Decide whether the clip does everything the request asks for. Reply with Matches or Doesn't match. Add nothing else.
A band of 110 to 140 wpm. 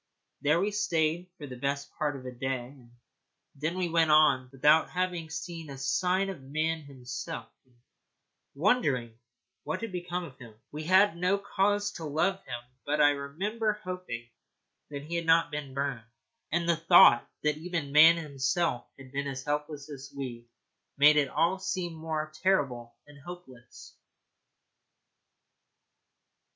Doesn't match